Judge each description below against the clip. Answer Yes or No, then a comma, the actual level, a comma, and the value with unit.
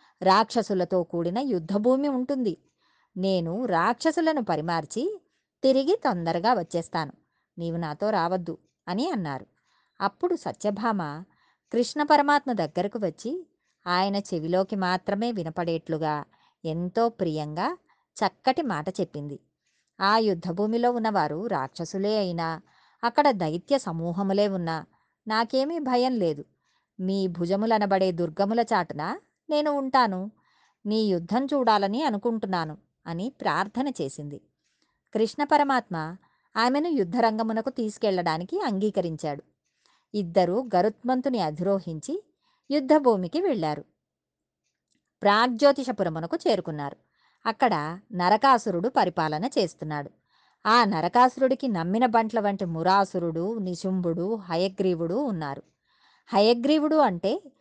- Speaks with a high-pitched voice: Yes, high, 200 Hz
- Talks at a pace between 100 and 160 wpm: No, average, 85 wpm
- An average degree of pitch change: No, wide, 6.4 semitones